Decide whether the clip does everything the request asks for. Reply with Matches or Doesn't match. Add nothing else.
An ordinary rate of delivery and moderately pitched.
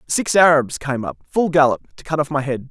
Doesn't match